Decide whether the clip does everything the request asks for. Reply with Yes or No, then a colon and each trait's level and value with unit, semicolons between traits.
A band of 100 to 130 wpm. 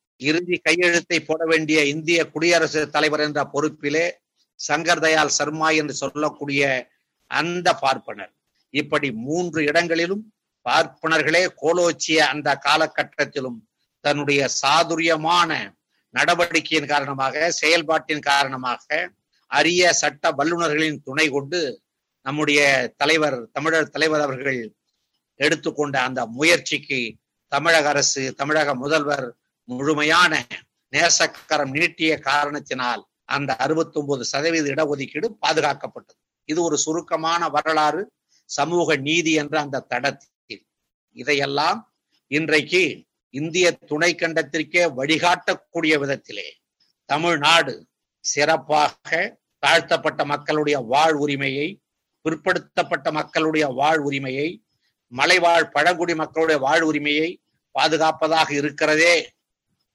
No: average, 90 wpm